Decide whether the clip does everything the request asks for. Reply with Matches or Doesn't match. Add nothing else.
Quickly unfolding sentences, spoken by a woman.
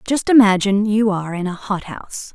Doesn't match